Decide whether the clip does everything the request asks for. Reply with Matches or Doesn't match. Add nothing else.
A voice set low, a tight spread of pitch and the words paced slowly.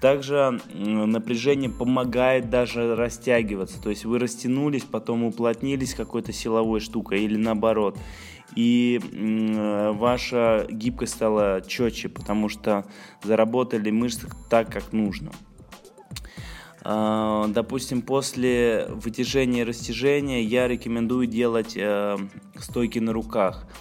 Matches